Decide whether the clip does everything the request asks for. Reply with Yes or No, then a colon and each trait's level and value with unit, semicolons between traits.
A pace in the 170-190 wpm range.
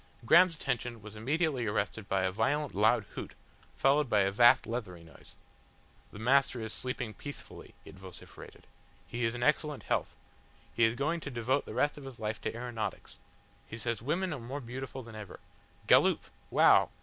Yes: average, 175 wpm